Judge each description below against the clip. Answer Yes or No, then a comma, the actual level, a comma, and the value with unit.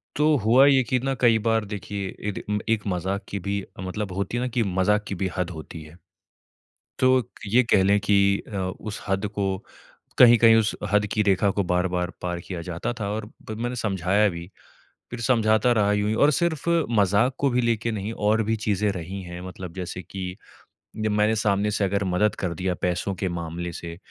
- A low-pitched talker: Yes, low, 100 Hz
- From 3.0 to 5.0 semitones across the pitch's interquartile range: Yes, average, 3.3 semitones